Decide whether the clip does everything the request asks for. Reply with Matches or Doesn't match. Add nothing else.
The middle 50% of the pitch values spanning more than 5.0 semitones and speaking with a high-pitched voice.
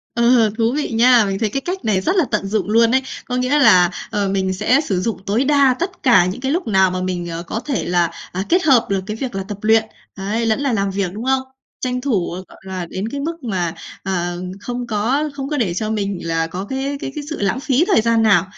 Matches